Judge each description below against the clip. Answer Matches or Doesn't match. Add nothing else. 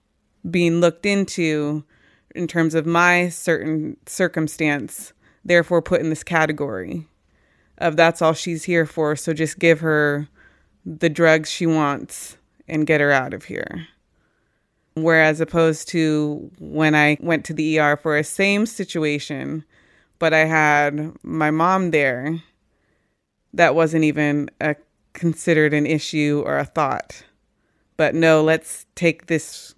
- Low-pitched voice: Doesn't match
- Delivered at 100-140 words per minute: Matches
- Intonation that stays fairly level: Matches